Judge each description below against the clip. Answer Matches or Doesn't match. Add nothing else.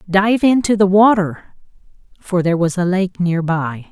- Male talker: Doesn't match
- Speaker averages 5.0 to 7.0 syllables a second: Doesn't match